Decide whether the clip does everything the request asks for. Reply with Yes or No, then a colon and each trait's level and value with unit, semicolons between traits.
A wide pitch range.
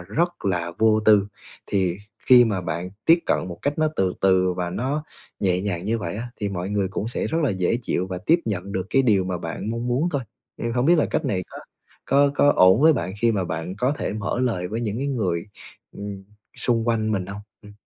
No: average, 4.8 semitones